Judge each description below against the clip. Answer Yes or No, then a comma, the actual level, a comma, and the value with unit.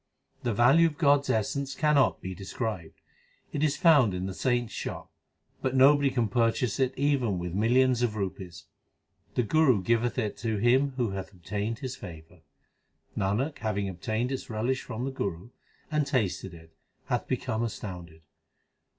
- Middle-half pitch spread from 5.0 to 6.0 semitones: Yes, average, 5.3 semitones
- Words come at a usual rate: Yes, average, 160 wpm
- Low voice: Yes, low, 115 Hz